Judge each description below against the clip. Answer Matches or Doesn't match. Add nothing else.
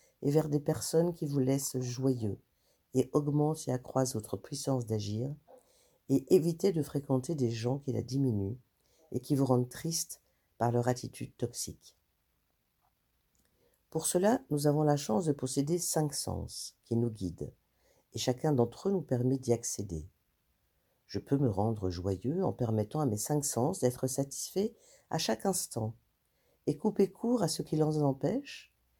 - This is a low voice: Matches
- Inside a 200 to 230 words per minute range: Doesn't match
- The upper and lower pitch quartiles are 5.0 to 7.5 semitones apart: Matches